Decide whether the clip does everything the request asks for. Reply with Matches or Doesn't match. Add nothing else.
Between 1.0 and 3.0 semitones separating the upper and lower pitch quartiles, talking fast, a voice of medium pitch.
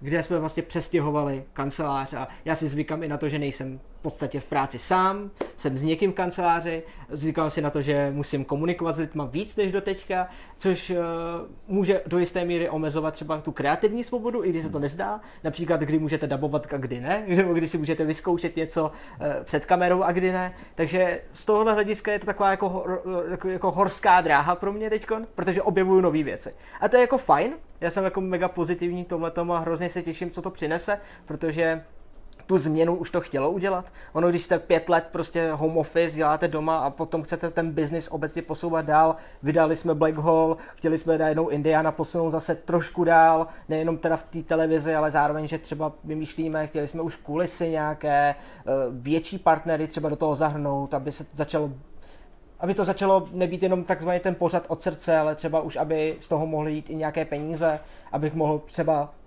Matches